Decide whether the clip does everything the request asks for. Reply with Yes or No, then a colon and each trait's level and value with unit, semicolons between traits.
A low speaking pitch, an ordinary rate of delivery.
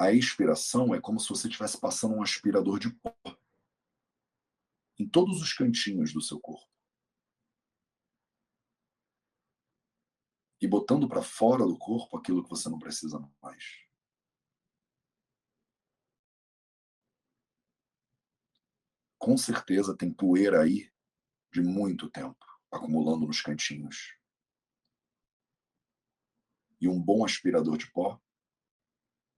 No: very low, 90 Hz; slow, 100 wpm